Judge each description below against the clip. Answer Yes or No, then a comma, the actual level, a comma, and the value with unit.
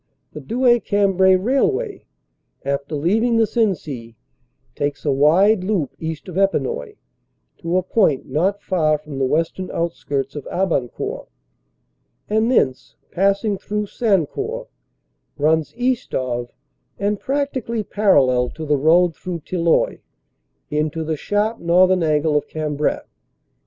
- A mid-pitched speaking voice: Yes, medium, 180 Hz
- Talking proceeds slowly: Yes, slow, 130 wpm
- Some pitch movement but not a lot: No, wide, 6.0 semitones